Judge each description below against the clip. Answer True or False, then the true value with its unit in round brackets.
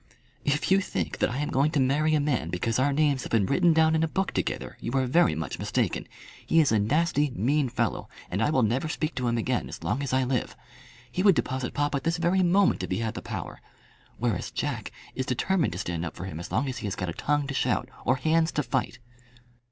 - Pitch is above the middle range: False (135 Hz)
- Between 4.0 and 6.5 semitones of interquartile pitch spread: True (5.1 semitones)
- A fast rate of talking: True (245 wpm)